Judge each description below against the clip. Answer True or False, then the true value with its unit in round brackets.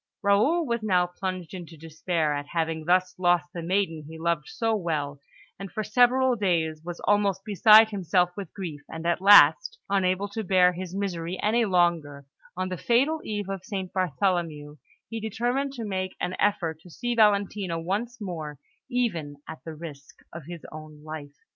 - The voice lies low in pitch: False (185 Hz)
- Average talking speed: True (170 wpm)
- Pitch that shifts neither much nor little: True (4.1 semitones)